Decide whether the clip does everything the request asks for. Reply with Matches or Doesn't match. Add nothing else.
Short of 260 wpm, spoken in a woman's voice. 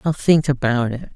Matches